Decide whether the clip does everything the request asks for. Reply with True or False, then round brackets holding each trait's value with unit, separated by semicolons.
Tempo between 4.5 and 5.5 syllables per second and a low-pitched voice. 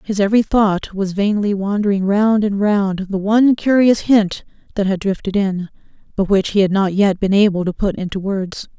False (5.0 syllables/s; 200 Hz)